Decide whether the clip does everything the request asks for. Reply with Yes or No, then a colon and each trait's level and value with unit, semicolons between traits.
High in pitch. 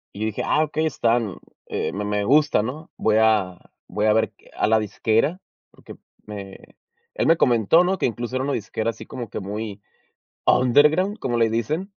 No: low, 115 Hz